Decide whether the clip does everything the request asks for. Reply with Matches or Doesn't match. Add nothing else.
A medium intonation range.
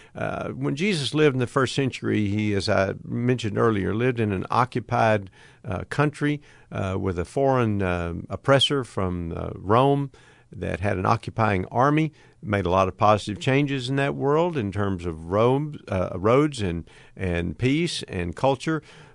Doesn't match